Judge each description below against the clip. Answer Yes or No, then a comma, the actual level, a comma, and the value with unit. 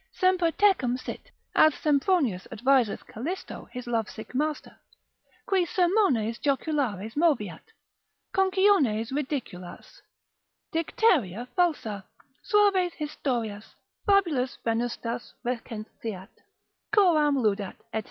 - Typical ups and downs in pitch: No, wide, 7.7 semitones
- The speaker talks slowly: Yes, slow, 85 wpm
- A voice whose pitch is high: Yes, very high, 270 Hz